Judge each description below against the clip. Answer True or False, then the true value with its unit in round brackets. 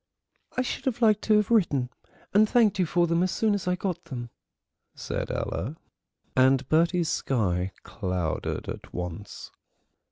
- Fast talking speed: False (155 wpm)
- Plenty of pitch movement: True (9.0 semitones)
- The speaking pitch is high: False (170 Hz)